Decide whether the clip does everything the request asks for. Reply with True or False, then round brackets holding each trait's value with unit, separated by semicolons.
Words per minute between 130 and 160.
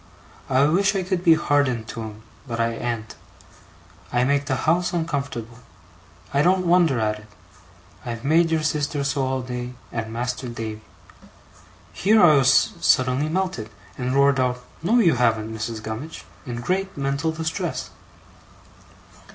True (150 wpm)